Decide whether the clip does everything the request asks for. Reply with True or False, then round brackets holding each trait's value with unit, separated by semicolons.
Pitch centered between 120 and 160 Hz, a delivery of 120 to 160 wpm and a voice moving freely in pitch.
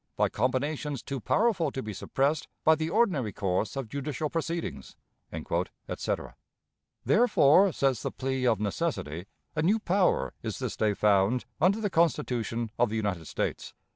True (135 Hz; 150 wpm; 7.0 semitones)